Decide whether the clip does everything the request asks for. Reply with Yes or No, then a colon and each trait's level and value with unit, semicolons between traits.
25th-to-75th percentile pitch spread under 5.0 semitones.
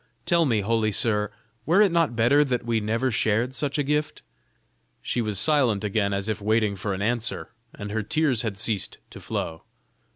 Yes: average, 4.3 semitones